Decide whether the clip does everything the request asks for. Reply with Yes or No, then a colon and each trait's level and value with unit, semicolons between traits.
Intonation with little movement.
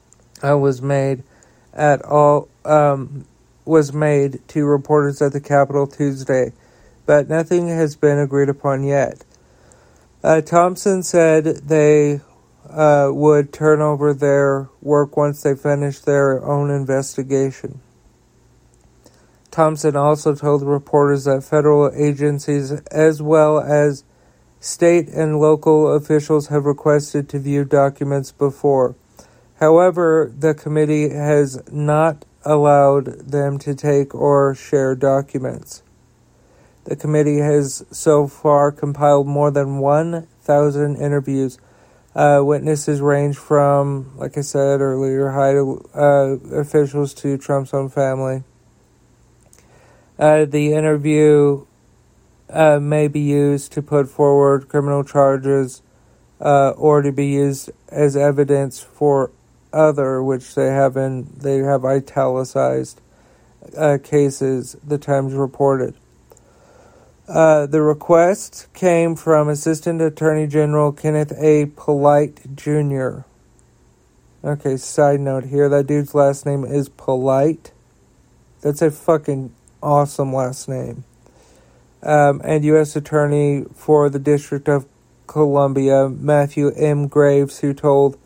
Yes: narrow, 1.5 semitones